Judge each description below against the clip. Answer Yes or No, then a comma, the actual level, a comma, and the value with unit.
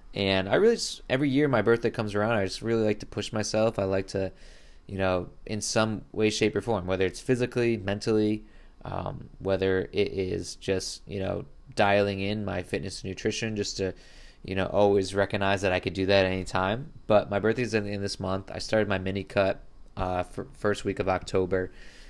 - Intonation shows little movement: Yes, narrow, 2.3 semitones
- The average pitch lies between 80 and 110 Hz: Yes, low, 100 Hz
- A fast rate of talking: Yes, fast, 210 wpm